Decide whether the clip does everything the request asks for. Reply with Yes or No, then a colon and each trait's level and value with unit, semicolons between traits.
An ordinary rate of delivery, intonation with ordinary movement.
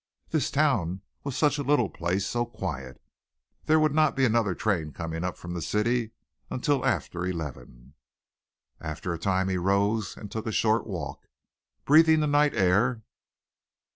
No: average, 160 wpm; wide, 7.3 semitones